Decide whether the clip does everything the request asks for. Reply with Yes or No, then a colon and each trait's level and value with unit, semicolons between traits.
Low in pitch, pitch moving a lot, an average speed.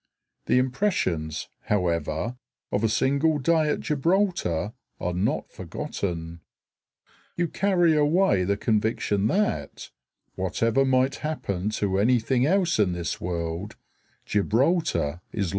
No: low, 110 Hz; wide, 8.9 semitones; slow, 125 wpm